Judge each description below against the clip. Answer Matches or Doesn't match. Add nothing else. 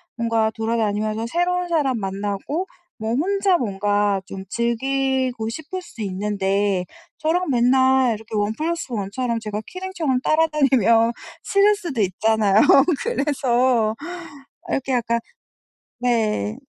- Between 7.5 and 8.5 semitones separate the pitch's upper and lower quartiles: Doesn't match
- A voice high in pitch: Matches